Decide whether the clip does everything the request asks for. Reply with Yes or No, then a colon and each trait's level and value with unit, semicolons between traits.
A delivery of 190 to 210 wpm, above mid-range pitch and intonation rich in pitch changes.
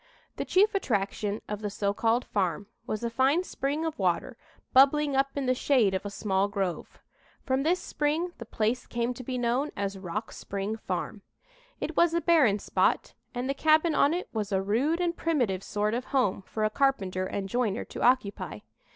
Yes: average, 195 wpm; high, 240 Hz; wide, 5.8 semitones